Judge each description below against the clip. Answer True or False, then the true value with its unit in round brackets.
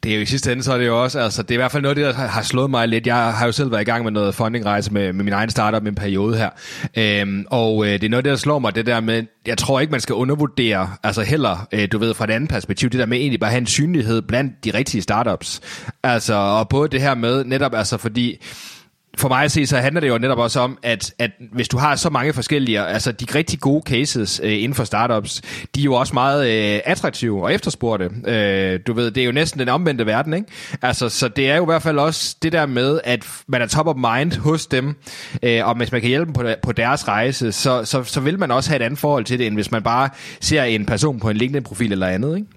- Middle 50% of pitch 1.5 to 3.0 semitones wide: False (3.8 semitones)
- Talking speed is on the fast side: True (275 wpm)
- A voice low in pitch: True (125 Hz)